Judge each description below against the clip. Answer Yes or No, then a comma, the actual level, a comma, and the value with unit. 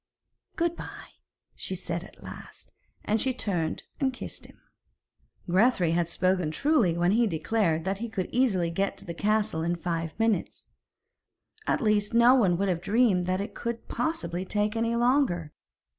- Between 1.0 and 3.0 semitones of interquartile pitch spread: No, average, 5.0 semitones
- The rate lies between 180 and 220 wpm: No, average, 165 wpm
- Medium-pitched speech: No, high, 200 Hz